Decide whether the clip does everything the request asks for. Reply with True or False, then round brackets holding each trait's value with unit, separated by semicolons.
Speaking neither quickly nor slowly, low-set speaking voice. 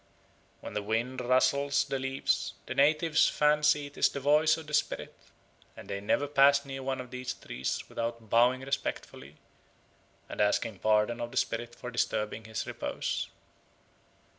True (160 wpm; 130 Hz)